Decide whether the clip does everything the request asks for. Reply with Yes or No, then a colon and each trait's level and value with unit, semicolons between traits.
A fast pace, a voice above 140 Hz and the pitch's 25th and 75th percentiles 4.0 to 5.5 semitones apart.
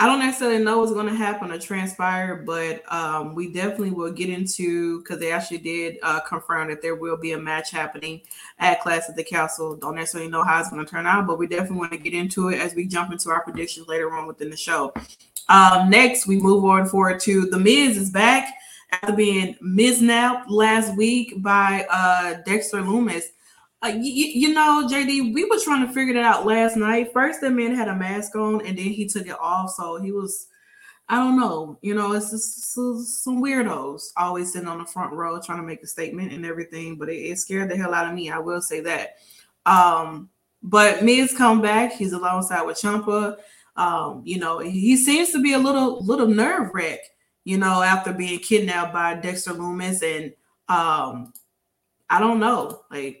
Yes: fast, 210 wpm; high, 190 Hz; average, 5.1 semitones